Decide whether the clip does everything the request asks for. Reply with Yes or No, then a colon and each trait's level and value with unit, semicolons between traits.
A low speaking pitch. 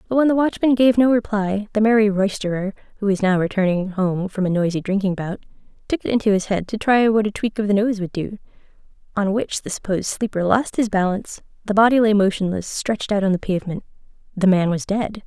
No: high, 205 Hz